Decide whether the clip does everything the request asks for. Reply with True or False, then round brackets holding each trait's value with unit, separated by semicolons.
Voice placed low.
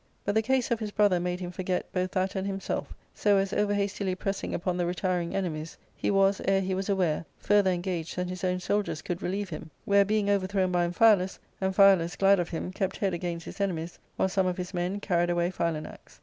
False (185 Hz)